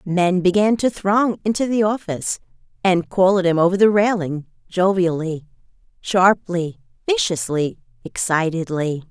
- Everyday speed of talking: No, slow, 120 wpm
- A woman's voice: Yes, female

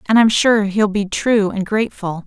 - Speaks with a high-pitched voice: Yes, high, 205 Hz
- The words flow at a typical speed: No, fast, 210 wpm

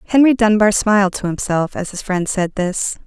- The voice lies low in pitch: No, high, 200 Hz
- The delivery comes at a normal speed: Yes, average, 195 wpm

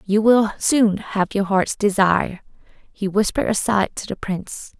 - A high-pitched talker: Yes, high, 205 Hz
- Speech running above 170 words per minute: No, average, 165 wpm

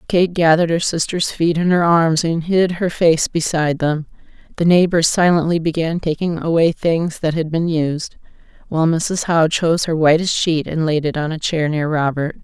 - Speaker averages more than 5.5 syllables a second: No, 5.0 syllables/s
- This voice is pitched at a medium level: Yes, medium, 165 Hz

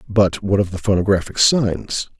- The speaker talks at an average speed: Yes, average, 165 wpm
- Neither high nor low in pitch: No, low, 100 Hz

